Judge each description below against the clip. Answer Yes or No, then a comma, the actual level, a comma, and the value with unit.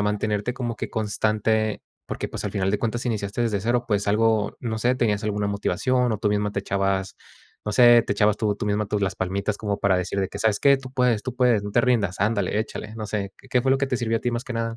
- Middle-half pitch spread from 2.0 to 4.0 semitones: Yes, average, 2.7 semitones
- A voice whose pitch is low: Yes, low, 105 Hz